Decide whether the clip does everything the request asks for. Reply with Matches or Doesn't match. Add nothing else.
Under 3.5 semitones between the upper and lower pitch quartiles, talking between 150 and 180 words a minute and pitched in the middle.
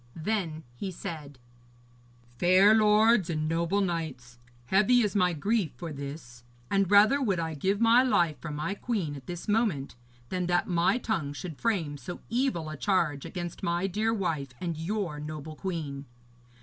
Doesn't match